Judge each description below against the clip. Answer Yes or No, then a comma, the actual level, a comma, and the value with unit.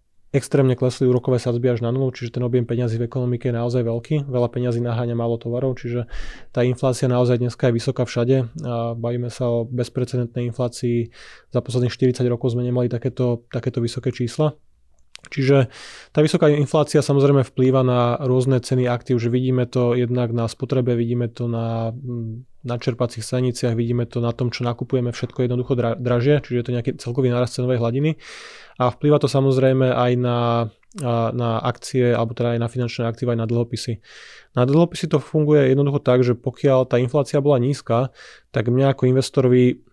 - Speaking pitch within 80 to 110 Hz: No, low, 125 Hz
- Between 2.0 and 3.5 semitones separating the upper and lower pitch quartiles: No, narrow, 1.6 semitones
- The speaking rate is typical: No, fast, 175 wpm